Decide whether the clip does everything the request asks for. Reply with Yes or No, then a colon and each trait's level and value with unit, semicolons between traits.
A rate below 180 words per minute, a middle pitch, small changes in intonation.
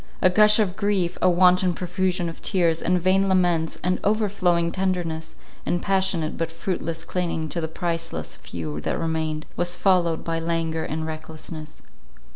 Yes: average, 155 wpm; medium, 175 Hz; narrow, 2.3 semitones